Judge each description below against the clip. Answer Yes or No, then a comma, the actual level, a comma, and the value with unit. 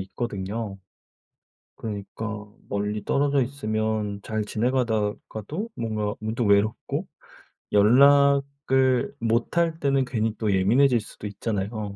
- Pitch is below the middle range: Yes, low, 110 Hz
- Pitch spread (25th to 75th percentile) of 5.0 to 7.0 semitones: No, average, 4.2 semitones